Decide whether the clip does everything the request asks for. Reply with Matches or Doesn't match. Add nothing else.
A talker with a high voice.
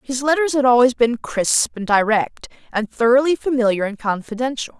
Matches